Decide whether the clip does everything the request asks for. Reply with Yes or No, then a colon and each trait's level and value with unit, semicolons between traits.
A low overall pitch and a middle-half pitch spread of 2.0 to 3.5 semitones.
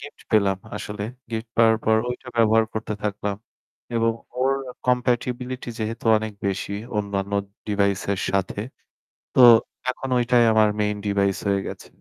Yes: low, 110 Hz; average, 2.8 semitones